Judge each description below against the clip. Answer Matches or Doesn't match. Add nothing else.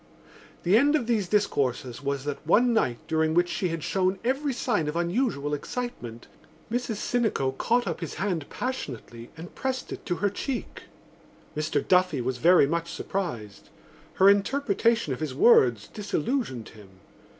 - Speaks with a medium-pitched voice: Matches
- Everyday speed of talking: Matches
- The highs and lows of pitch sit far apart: Matches